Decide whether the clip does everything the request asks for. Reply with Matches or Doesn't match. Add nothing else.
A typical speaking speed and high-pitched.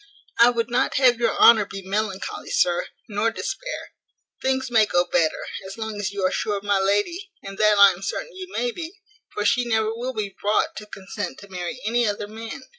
Doesn't match